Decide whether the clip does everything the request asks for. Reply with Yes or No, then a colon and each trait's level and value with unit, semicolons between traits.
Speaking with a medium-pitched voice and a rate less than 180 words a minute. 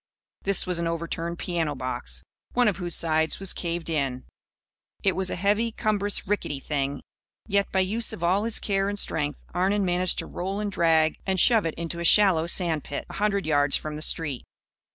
No: medium, 175 Hz; average, 195 wpm